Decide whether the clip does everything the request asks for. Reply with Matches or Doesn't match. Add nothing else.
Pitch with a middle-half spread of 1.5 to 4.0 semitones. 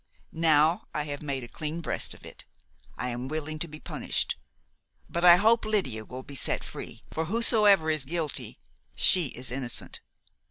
Doesn't match